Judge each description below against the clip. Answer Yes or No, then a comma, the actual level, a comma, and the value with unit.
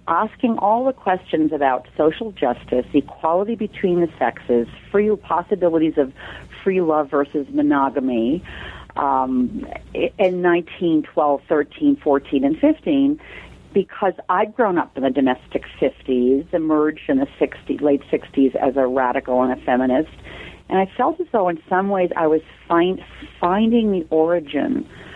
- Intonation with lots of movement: Yes, wide, 6.5 semitones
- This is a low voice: No, medium, 165 Hz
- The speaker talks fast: No, average, 140 wpm